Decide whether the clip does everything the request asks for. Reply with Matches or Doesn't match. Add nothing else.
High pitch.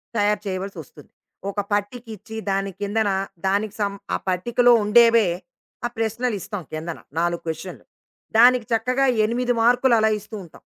Matches